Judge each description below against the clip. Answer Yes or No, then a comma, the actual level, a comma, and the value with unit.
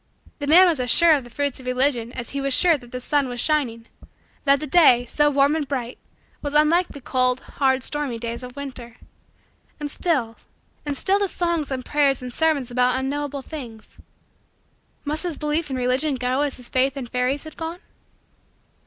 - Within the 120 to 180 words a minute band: No, average, 195 wpm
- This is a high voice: Yes, very high, 275 Hz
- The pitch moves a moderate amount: Yes, average, 3.0 semitones